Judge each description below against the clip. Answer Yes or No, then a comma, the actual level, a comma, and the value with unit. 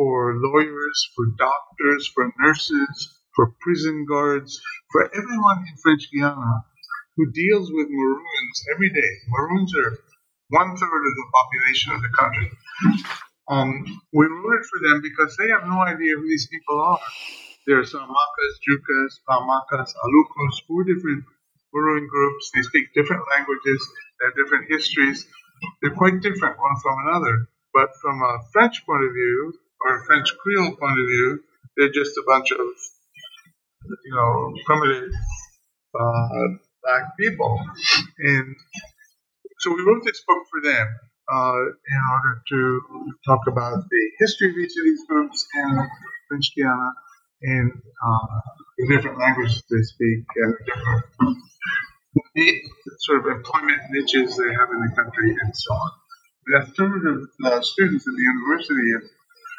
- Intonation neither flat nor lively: No, wide, 7.7 semitones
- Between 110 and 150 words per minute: Yes, average, 145 wpm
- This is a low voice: No, medium, 145 Hz